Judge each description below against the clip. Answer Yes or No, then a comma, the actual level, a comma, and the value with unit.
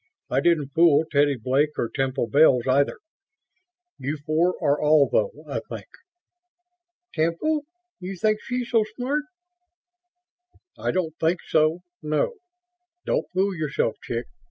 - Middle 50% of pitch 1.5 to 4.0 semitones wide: No, average, 4.6 semitones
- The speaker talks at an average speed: No, slow, 130 wpm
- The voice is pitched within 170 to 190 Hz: No, medium, 155 Hz